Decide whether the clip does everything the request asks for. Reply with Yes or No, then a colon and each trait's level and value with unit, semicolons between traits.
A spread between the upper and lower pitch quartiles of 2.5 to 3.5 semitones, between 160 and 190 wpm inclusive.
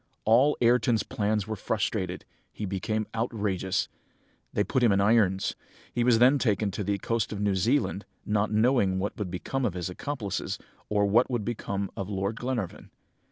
Yes: average, 3.0 semitones; average, 170 wpm